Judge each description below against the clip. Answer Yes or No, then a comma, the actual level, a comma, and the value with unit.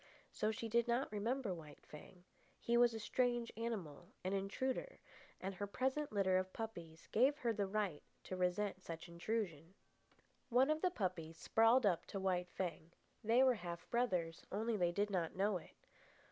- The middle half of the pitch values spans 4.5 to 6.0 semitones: Yes, average, 4.8 semitones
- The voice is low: No, high, 200 Hz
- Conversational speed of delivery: Yes, average, 175 wpm